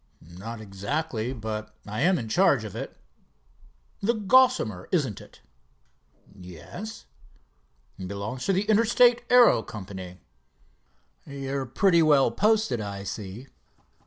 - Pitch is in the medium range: No, low, 125 Hz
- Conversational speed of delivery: No, slow, 110 wpm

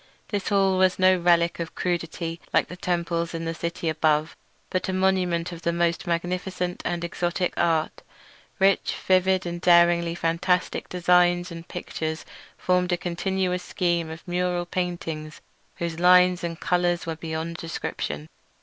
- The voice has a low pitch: No, medium, 175 Hz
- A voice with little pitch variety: Yes, narrow, 1.3 semitones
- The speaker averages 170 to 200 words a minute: No, average, 150 wpm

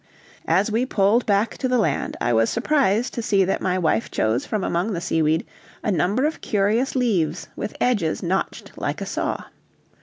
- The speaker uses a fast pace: No, average, 185 wpm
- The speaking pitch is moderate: No, high, 200 Hz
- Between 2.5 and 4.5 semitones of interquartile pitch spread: No, average, 5.2 semitones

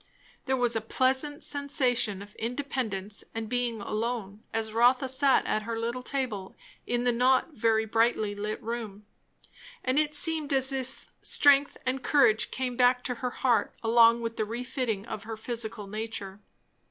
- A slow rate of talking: No, average, 160 wpm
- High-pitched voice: Yes, high, 235 Hz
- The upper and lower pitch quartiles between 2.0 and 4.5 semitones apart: Yes, average, 3.0 semitones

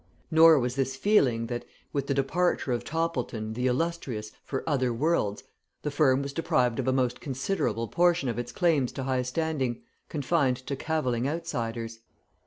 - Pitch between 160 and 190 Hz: No, low, 135 Hz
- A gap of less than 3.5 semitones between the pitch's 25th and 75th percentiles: No, average, 4.7 semitones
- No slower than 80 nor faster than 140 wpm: No, average, 165 wpm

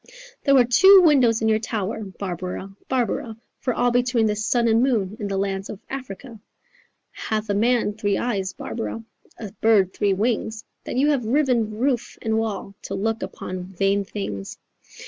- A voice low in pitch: No, high, 220 Hz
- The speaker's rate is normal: Yes, average, 170 wpm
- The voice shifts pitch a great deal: No, average, 3.6 semitones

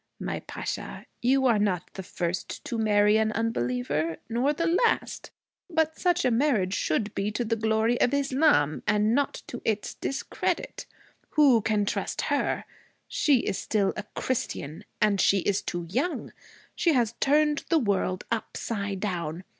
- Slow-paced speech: No, average, 155 wpm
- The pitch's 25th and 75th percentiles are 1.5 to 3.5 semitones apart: No, wide, 5.4 semitones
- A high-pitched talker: Yes, high, 220 Hz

